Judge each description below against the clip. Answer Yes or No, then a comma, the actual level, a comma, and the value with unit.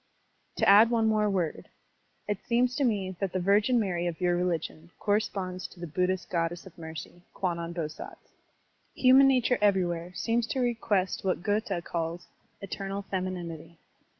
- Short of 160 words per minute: Yes, average, 150 wpm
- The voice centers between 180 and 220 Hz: Yes, medium, 185 Hz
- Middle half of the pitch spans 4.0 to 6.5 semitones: No, average, 3.6 semitones